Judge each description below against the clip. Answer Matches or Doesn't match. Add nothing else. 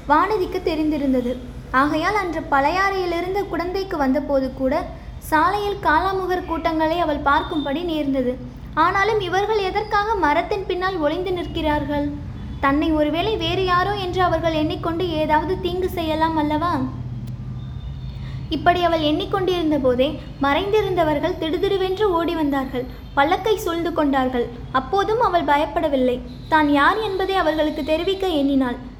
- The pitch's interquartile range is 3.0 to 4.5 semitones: Matches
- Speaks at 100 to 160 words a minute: Matches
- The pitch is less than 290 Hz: Doesn't match